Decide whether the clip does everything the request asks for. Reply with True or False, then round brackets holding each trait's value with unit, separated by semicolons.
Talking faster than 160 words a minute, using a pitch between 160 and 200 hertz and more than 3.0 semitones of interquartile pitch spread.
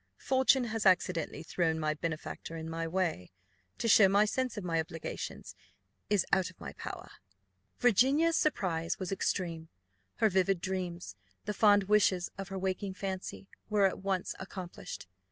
False (155 wpm; 190 Hz; 3.5 semitones)